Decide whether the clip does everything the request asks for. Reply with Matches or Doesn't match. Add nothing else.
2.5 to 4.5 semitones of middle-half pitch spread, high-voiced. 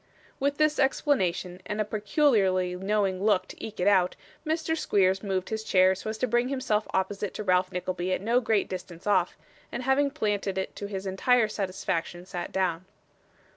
Matches